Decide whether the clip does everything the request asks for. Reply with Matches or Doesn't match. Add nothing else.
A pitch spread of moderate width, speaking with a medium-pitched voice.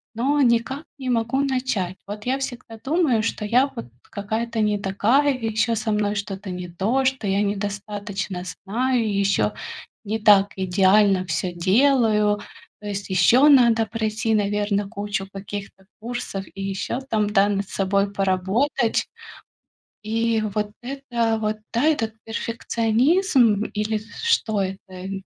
Doesn't match